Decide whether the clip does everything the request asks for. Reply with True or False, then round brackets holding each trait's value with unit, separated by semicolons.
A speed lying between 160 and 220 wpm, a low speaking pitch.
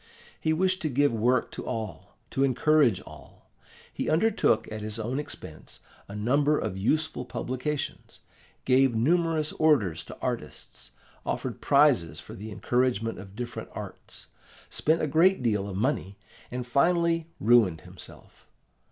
False (140 wpm; 125 Hz)